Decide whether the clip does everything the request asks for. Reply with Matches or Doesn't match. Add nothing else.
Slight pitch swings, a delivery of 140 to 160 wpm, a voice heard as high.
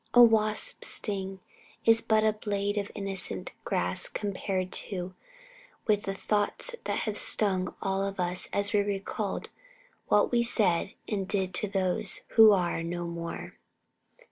Matches